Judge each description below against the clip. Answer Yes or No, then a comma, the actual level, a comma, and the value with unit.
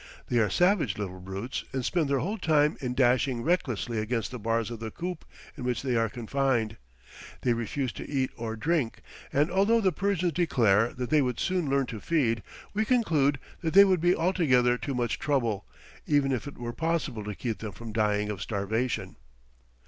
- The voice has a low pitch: Yes, low, 130 Hz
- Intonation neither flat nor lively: No, wide, 5.8 semitones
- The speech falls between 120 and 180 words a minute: No, average, 195 wpm